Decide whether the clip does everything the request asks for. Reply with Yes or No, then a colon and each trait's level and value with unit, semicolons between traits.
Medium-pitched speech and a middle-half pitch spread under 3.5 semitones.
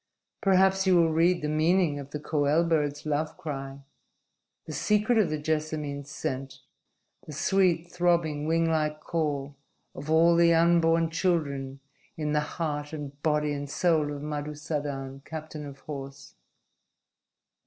Yes: medium, 155 Hz; narrow, 2.5 semitones